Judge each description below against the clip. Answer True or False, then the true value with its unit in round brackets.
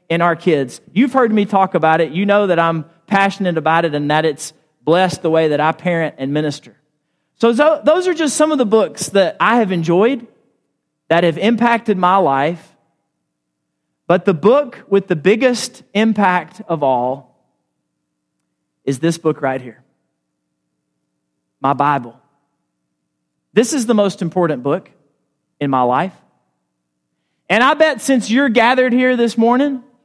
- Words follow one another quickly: False (155 wpm)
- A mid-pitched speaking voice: True (165 Hz)